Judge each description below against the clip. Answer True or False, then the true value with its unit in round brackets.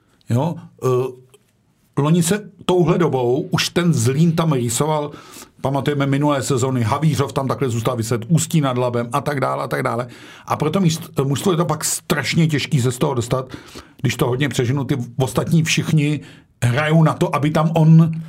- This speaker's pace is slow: False (170 wpm)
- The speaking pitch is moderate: True (145 Hz)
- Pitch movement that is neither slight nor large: True (3.8 semitones)